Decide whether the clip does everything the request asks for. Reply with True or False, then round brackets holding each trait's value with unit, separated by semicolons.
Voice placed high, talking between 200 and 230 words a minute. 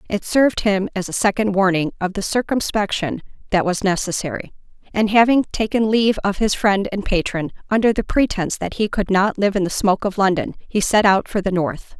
True (200 Hz; 205 wpm)